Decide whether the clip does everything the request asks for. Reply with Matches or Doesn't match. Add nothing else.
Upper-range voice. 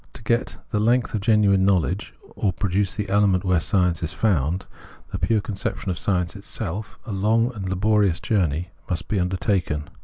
Doesn't match